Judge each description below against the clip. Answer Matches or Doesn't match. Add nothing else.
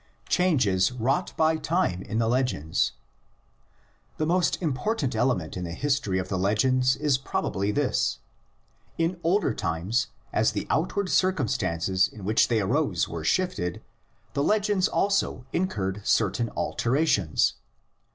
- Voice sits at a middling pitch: Doesn't match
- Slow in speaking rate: Matches